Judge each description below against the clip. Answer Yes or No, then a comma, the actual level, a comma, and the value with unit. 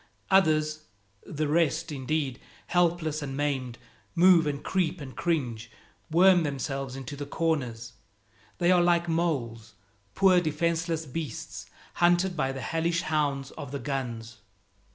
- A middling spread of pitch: Yes, average, 3.9 semitones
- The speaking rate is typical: No, slow, 130 wpm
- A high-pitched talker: No, medium, 155 Hz